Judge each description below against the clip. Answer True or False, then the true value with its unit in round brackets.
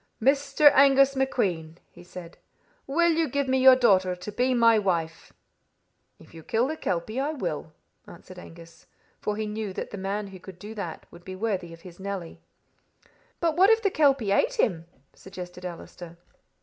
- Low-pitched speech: False (205 Hz)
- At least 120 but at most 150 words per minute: False (175 wpm)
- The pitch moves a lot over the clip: True (7.1 semitones)